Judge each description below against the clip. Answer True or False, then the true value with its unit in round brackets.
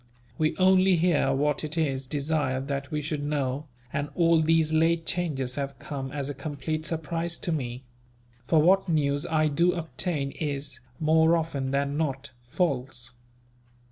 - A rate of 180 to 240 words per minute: False (155 wpm)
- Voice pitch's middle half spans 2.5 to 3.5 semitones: True (2.9 semitones)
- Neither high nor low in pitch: True (150 Hz)